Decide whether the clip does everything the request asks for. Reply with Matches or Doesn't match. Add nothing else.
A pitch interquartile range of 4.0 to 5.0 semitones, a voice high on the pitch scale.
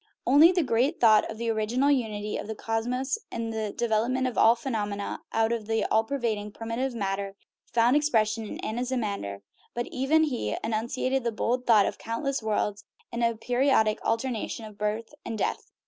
Doesn't match